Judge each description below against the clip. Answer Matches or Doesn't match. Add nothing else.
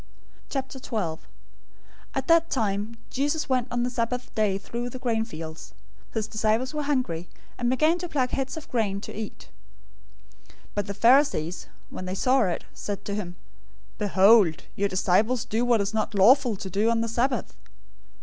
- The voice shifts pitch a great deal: Doesn't match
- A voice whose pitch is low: Doesn't match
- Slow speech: Doesn't match